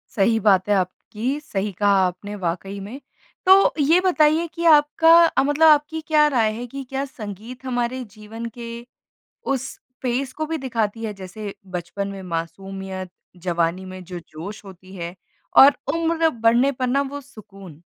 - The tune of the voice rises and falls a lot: Yes, wide, 6.4 semitones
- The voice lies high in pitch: Yes, high, 225 Hz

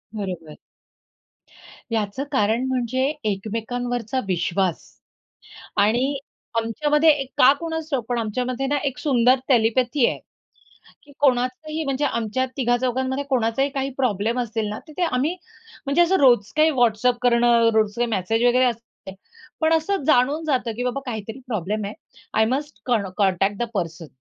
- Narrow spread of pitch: No, average, 3.7 semitones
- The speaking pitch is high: Yes, high, 245 Hz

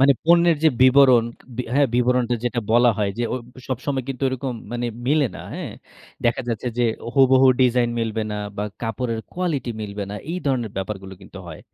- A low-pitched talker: Yes, low, 125 Hz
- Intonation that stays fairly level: No, average, 3.0 semitones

